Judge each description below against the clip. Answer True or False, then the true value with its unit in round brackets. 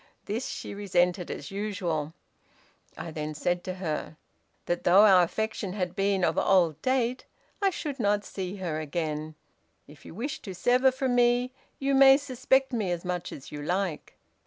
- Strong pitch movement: True (6.0 semitones)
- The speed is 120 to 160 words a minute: False (170 wpm)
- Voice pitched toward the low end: False (195 Hz)